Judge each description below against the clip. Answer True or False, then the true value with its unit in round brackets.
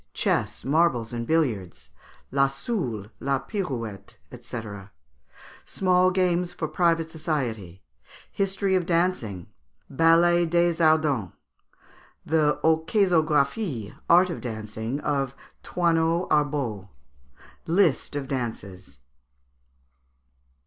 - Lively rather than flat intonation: True (6.4 semitones)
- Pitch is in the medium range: True (155 Hz)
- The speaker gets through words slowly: True (90 wpm)